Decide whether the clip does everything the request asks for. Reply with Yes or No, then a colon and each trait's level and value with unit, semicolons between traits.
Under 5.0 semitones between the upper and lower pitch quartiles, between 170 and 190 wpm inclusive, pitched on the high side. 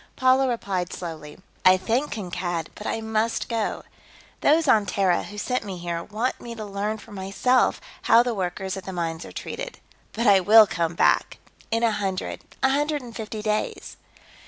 Yes: average, 3.9 semitones; average, 180 wpm; high, 210 Hz